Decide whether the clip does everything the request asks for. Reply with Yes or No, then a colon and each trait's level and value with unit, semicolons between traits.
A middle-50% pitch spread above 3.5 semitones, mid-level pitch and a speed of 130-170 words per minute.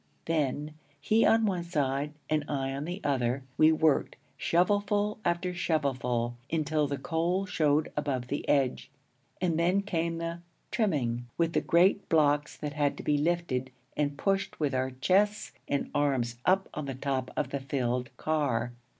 Yes: average, 4.2 semitones; medium, 150 Hz; average, 160 wpm